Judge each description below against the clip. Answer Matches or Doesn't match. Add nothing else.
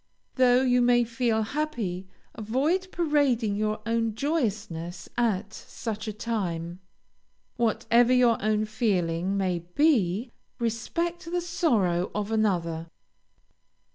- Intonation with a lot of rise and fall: Doesn't match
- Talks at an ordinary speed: Doesn't match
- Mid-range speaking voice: Doesn't match